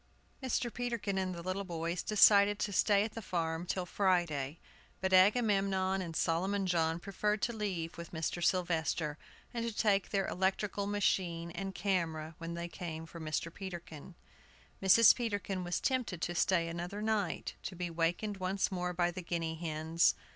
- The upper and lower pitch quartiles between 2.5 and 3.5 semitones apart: Yes, average, 3.1 semitones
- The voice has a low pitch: No, medium, 185 Hz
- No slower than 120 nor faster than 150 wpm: No, average, 165 wpm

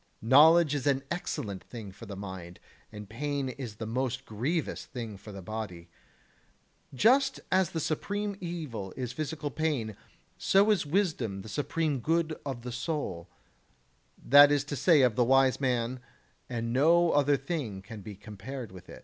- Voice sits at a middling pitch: No, low, 130 Hz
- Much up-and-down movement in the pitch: Yes, wide, 6.0 semitones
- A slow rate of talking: No, average, 165 wpm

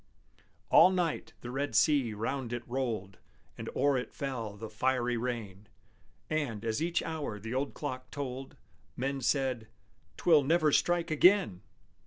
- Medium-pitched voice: No, low, 130 Hz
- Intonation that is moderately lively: Yes, average, 4.2 semitones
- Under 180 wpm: Yes, average, 145 wpm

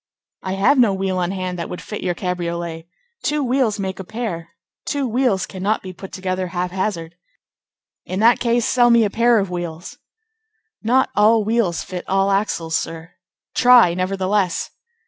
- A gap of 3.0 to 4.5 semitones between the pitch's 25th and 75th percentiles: Yes, average, 4.1 semitones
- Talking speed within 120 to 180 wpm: Yes, average, 165 wpm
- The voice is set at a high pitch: Yes, high, 195 Hz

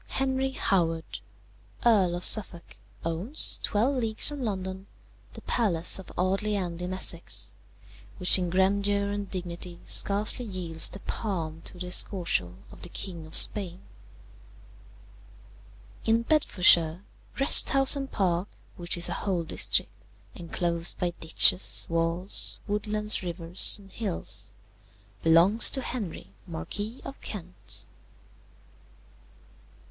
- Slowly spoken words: Yes, slow, 120 wpm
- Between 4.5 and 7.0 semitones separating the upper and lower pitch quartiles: No, average, 3.6 semitones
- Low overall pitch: No, medium, 185 Hz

